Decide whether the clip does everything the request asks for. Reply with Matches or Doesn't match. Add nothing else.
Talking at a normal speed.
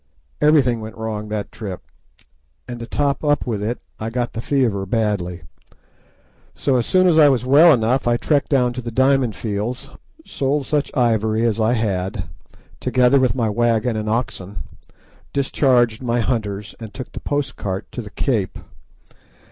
Matches